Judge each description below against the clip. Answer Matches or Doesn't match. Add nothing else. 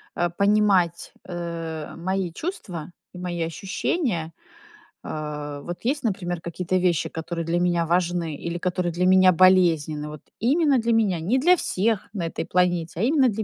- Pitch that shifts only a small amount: Doesn't match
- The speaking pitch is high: Doesn't match